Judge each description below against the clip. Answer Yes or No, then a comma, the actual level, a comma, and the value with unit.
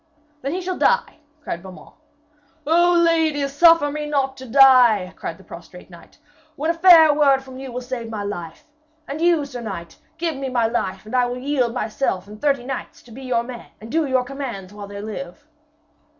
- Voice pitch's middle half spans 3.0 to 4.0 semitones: No, average, 4.8 semitones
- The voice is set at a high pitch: Yes, very high, 260 Hz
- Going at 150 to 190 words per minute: No, average, 200 wpm